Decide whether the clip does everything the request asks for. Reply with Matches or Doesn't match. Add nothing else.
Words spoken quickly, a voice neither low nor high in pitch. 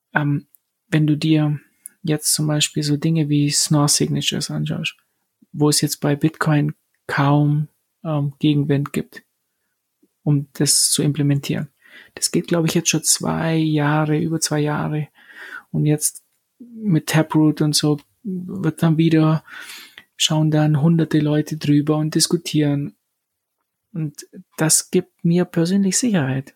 Doesn't match